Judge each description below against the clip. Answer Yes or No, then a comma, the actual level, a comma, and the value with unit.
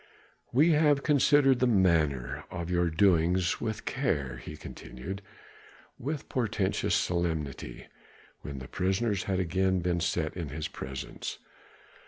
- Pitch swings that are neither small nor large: No, wide, 6.1 semitones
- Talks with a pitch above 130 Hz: No, very low, 90 Hz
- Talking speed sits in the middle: No, slow, 125 wpm